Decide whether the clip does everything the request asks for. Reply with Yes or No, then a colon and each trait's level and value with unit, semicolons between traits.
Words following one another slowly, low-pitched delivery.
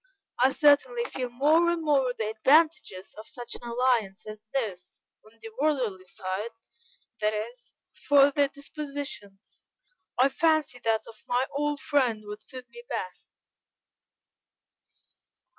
No: slow, 130 wpm; very high, 255 Hz